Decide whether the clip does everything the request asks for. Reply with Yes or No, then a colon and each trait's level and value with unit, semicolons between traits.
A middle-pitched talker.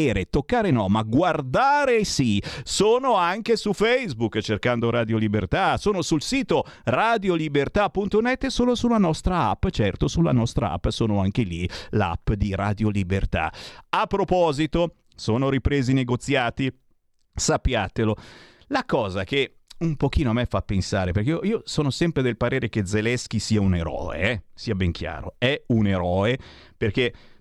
No: low, 125 Hz